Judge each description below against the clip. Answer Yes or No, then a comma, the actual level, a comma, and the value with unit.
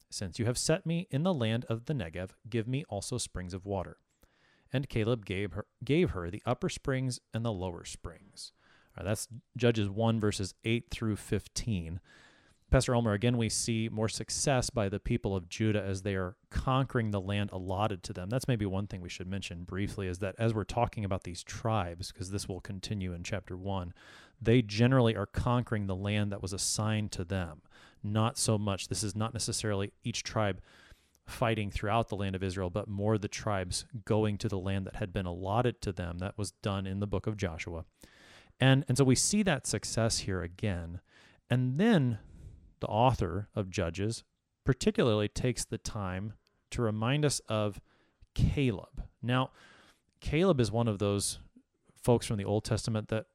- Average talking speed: Yes, average, 185 wpm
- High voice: No, low, 105 Hz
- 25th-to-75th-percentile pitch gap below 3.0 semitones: No, average, 3.4 semitones